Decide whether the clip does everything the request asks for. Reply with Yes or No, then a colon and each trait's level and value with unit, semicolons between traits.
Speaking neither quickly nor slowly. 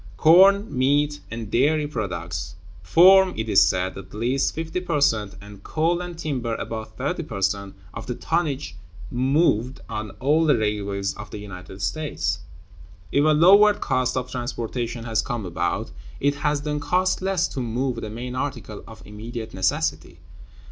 Yes: average, 160 wpm